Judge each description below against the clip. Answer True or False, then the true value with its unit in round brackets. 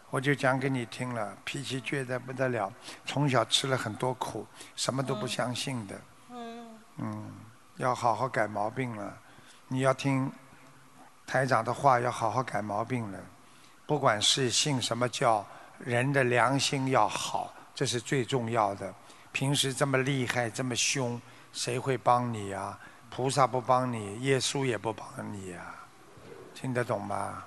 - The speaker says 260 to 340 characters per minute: False (220 characters per minute)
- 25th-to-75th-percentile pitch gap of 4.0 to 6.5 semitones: False (3.0 semitones)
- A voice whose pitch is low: True (125 Hz)